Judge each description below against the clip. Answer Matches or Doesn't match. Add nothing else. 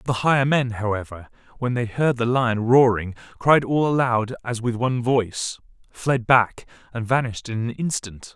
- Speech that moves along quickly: Doesn't match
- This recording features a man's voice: Matches